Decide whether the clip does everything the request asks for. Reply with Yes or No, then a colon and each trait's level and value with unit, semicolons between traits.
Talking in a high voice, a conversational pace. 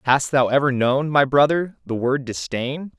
No: low, 135 Hz; average, 180 wpm